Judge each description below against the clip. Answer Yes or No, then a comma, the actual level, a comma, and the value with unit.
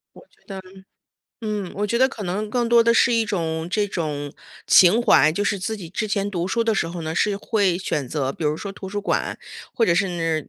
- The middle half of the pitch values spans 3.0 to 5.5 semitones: Yes, average, 4.3 semitones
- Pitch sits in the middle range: No, high, 195 Hz